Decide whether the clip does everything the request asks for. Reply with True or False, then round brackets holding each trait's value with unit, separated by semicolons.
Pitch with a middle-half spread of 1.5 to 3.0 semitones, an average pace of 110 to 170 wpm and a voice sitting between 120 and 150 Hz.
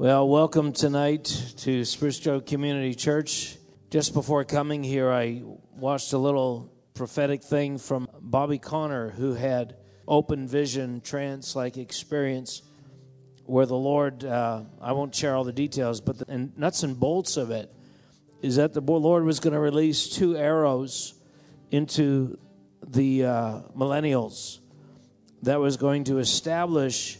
True (2.4 semitones; 135 wpm; 135 Hz)